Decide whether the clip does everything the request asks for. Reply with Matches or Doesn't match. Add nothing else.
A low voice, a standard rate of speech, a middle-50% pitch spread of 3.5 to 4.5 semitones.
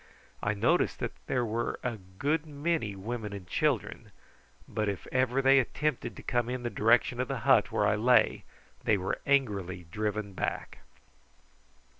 Matches